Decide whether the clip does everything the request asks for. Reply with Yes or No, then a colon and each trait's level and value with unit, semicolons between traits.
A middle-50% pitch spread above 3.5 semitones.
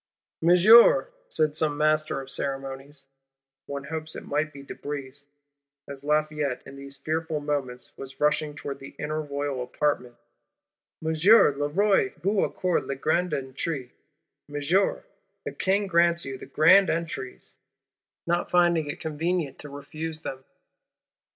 No: average, 3.0 semitones